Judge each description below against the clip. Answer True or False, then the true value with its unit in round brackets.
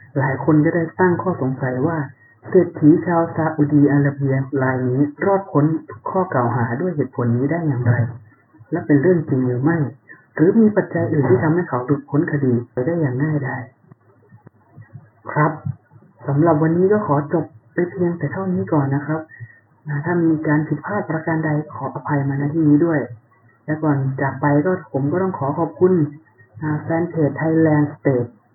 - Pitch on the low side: False (145 Hz)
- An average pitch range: True (3.8 semitones)